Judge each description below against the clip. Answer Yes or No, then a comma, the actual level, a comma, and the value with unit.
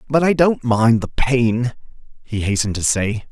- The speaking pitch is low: Yes, low, 120 Hz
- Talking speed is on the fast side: No, average, 180 wpm